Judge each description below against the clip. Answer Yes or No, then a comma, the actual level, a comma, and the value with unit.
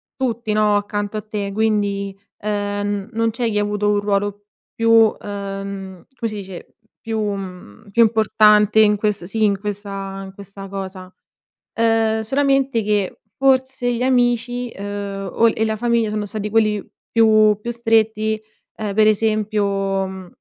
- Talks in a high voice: Yes, high, 210 Hz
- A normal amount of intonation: No, narrow, 2.0 semitones